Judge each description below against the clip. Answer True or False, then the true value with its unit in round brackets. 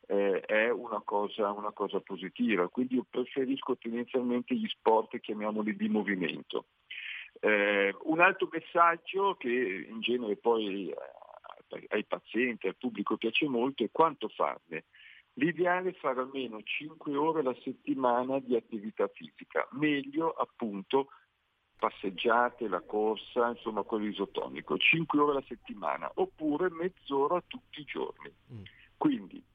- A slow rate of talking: False (125 wpm)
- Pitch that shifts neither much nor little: False (7.0 semitones)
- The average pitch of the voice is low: True (125 Hz)